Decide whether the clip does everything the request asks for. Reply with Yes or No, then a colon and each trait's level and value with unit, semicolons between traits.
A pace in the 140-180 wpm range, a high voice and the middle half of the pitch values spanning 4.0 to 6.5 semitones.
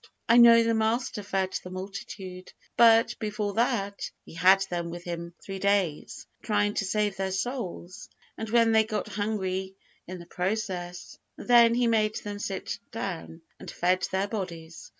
No: average, 160 wpm; high, 200 Hz; average, 3.2 semitones